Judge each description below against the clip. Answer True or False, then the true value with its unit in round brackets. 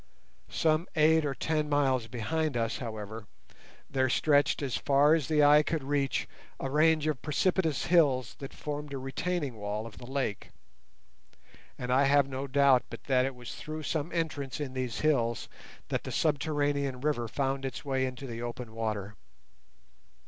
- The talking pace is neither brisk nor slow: True (165 wpm)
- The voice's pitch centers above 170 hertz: False (135 Hz)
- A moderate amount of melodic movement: True (3.2 semitones)